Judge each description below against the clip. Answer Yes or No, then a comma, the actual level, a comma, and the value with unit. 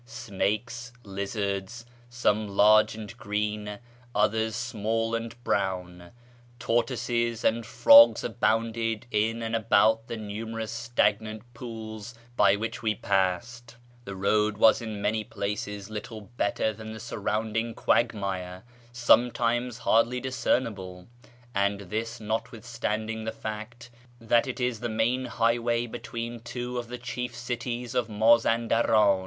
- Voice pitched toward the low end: Yes, low, 115 Hz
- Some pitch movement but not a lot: No, narrow, 2.0 semitones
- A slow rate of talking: Yes, slow, 125 wpm